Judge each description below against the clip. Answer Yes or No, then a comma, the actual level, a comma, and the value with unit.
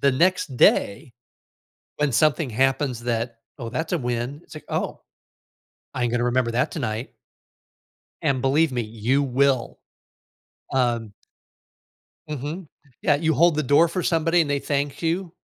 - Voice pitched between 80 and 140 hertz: Yes, low, 135 Hz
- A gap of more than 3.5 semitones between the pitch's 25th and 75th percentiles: Yes, average, 4.2 semitones